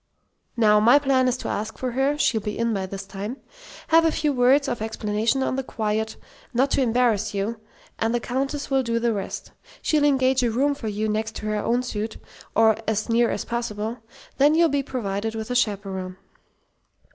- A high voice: Yes, high, 230 Hz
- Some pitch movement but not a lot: Yes, average, 3.7 semitones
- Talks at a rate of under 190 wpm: No, average, 200 wpm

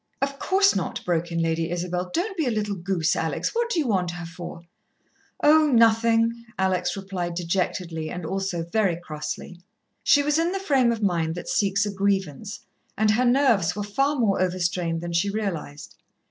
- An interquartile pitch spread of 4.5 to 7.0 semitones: Yes, average, 5.1 semitones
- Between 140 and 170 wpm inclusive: No, average, 180 wpm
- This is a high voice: Yes, high, 195 Hz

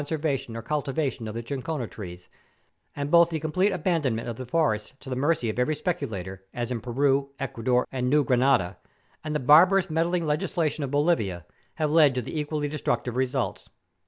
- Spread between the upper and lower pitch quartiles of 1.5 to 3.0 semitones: No, average, 4.3 semitones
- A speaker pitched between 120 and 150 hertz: Yes, medium, 140 Hz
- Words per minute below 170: No, average, 185 wpm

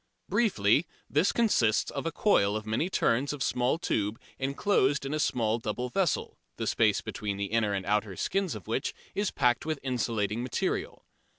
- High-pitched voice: No, low, 125 Hz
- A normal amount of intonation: No, wide, 6.3 semitones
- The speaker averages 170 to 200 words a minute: Yes, average, 175 wpm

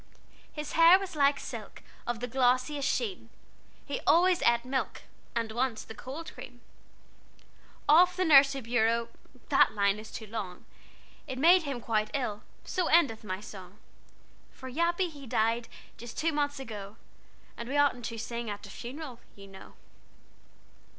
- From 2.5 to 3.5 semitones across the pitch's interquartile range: No, average, 5.0 semitones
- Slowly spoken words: No, average, 155 wpm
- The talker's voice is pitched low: No, very high, 250 Hz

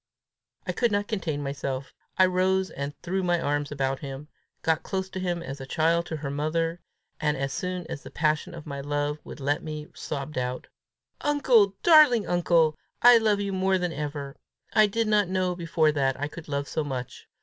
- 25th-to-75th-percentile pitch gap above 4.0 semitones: Yes, average, 4.6 semitones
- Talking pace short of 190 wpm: No, average, 195 wpm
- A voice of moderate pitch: Yes, medium, 160 Hz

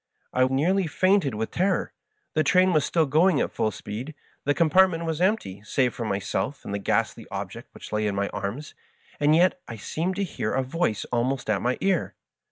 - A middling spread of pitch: No, wide, 7.4 semitones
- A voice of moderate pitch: Yes, medium, 145 Hz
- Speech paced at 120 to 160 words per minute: No, fast, 205 wpm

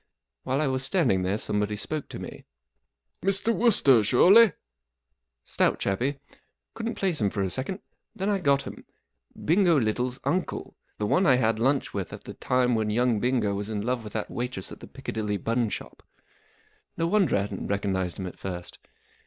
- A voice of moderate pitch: No, low, 125 Hz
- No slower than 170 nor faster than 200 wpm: Yes, average, 195 wpm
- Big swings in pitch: Yes, wide, 6.9 semitones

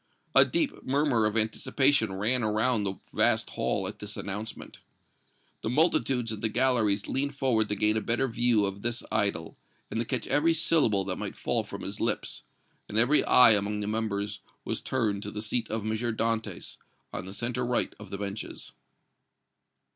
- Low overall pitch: Yes, low, 110 Hz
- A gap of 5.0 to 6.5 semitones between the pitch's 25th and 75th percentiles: No, average, 3.1 semitones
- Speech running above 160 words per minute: Yes, average, 180 wpm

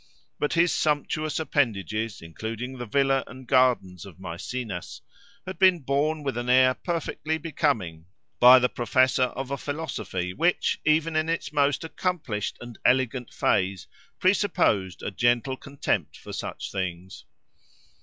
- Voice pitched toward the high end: No, low, 130 Hz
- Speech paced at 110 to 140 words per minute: Yes, slow, 135 wpm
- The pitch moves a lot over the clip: Yes, wide, 6.2 semitones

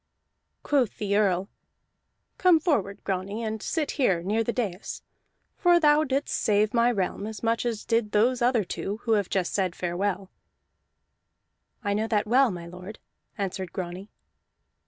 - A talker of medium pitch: No, high, 210 Hz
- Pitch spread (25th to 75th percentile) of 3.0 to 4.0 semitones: Yes, average, 3.7 semitones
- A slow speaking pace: No, average, 150 wpm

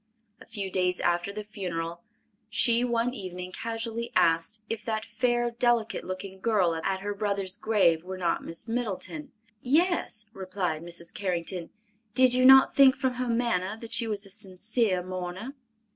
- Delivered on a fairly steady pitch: No, average, 4.3 semitones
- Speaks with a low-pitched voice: No, high, 205 Hz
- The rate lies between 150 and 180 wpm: Yes, average, 160 wpm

